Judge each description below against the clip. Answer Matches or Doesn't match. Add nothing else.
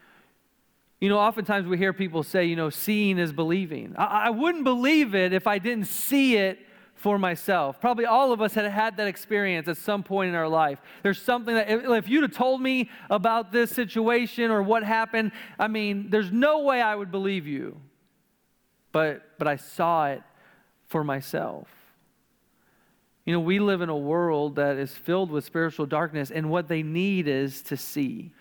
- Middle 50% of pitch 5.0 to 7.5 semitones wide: Matches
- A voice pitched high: Matches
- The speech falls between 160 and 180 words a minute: Doesn't match